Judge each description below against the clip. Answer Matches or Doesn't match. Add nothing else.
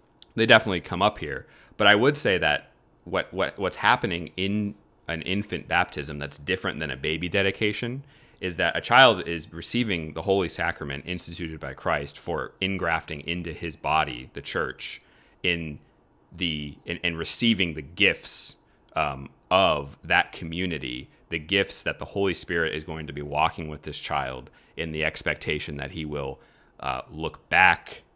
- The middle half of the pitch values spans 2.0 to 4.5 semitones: Matches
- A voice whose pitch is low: Matches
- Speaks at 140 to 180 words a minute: Matches